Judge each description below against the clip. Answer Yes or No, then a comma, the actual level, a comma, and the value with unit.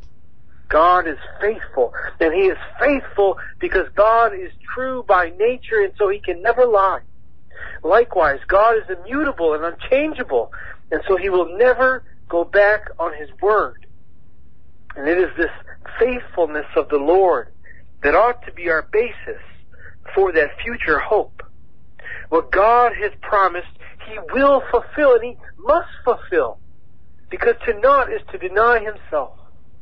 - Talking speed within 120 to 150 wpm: Yes, average, 145 wpm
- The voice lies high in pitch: Yes, high, 230 Hz